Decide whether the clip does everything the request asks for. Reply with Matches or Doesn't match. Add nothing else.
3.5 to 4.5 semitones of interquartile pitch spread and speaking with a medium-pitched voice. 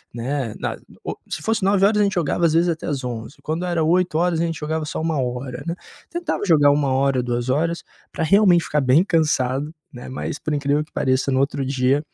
Matches